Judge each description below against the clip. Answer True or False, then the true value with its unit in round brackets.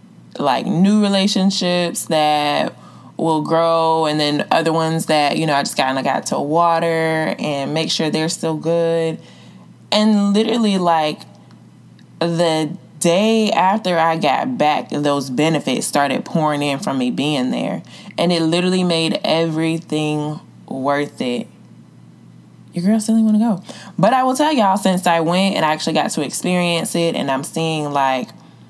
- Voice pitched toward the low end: False (165 Hz)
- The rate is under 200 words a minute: True (160 wpm)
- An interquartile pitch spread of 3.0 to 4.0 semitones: True (3.6 semitones)